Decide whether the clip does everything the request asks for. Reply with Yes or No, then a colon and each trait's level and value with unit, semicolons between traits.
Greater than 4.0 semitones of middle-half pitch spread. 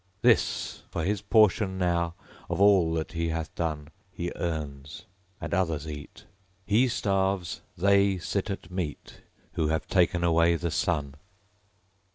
No: average, 3.2 semitones